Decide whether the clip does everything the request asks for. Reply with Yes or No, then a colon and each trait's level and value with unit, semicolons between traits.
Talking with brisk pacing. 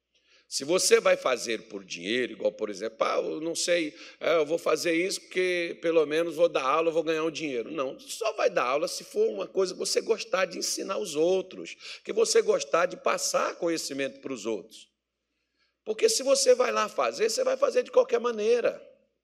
Yes: fast, 195 wpm